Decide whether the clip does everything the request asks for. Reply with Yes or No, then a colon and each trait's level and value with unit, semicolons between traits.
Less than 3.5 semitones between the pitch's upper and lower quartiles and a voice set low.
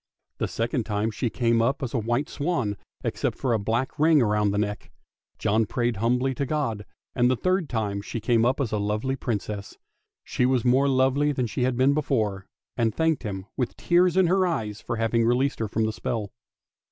No: average, 3.8 semitones; low, 120 Hz